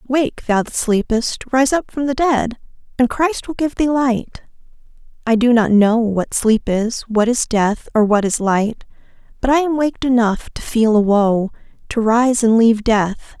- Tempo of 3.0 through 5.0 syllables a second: Yes, 4.4 syllables/s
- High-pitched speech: Yes, high, 235 Hz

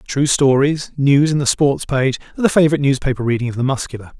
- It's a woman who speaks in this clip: No, male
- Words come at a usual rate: No, fast, 215 wpm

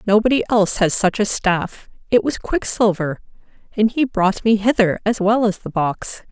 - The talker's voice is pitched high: Yes, high, 210 Hz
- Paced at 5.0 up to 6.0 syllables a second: No, 4.7 syllables/s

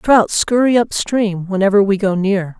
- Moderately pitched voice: No, high, 205 Hz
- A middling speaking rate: Yes, average, 185 wpm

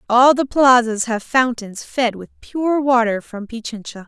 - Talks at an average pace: Yes, average, 160 wpm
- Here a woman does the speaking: Yes, female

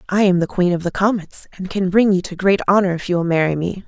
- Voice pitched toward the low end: No, medium, 185 Hz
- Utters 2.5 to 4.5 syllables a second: No, 6.2 syllables/s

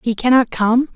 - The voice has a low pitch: No, high, 240 Hz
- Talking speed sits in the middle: Yes, average, 190 wpm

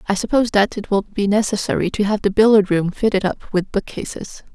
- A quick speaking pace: Yes, fast, 225 wpm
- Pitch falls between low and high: No, high, 205 Hz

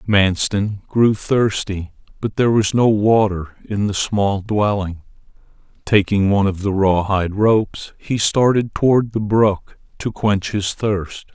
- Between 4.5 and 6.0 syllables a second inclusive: No, 4.0 syllables/s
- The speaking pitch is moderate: No, low, 105 Hz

